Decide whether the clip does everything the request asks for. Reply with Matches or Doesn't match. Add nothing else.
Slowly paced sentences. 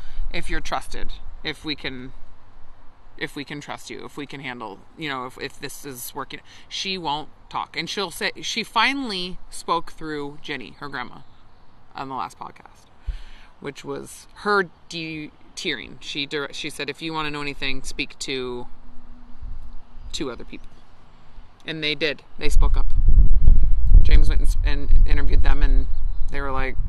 Doesn't match